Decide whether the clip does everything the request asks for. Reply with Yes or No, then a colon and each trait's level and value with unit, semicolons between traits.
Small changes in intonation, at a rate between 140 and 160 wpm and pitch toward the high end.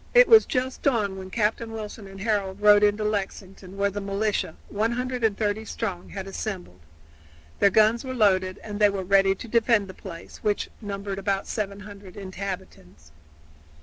Yes: narrow, 2.0 semitones; average, 155 wpm; high, 205 Hz